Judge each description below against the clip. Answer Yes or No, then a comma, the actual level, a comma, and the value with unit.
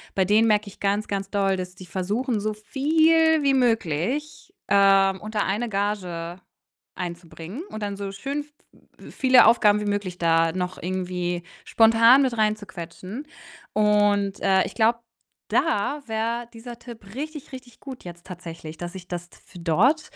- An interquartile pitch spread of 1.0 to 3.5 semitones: No, average, 4.5 semitones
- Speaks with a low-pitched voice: No, high, 205 Hz